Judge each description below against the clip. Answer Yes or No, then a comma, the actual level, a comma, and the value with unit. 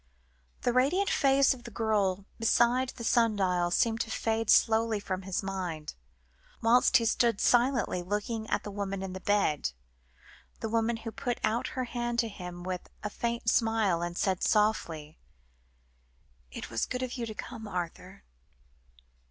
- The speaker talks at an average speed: Yes, average, 160 wpm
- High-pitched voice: Yes, high, 220 Hz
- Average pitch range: Yes, average, 3.9 semitones